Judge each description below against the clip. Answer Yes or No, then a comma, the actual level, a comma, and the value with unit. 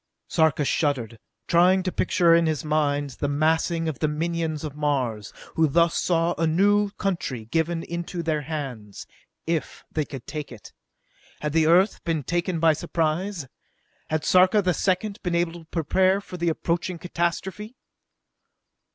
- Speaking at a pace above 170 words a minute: No, average, 155 wpm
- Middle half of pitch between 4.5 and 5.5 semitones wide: No, narrow, 2.6 semitones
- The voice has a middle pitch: Yes, medium, 165 Hz